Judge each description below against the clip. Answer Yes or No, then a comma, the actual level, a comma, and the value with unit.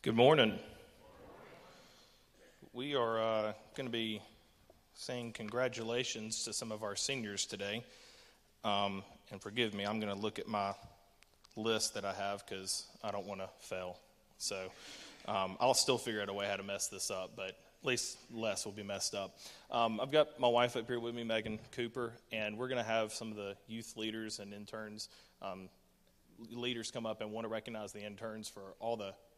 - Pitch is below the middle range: Yes, low, 110 Hz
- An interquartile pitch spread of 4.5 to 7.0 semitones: No, narrow, 2.5 semitones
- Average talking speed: Yes, average, 190 wpm